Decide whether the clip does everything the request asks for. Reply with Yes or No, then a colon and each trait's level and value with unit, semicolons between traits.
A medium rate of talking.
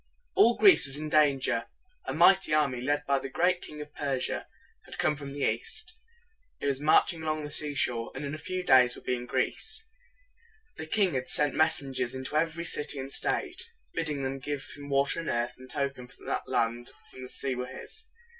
No: fast, 210 wpm